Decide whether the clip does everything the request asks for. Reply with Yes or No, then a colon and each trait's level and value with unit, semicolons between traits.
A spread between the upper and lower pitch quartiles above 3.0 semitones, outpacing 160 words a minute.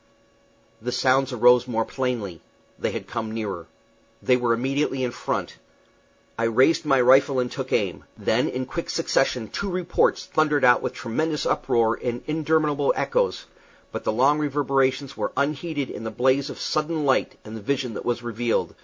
Yes: average, 3.5 semitones; average, 170 wpm